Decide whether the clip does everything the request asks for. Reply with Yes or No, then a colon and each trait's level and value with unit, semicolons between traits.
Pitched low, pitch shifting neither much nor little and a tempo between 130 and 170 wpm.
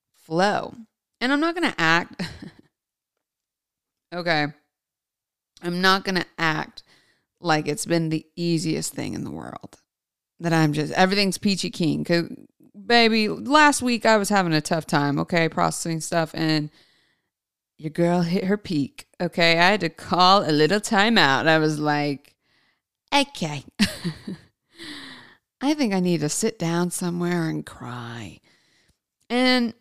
No: medium, 175 Hz; average, 4.8 semitones; average, 145 wpm